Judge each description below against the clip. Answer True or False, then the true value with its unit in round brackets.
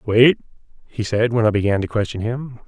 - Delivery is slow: False (200 wpm)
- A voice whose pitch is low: True (115 Hz)